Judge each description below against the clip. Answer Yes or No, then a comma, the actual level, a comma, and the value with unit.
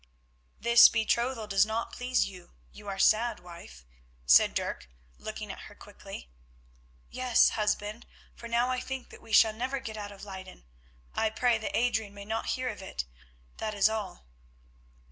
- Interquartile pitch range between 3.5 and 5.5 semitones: No, average, 2.9 semitones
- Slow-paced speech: No, average, 165 wpm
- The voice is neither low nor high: No, high, 220 Hz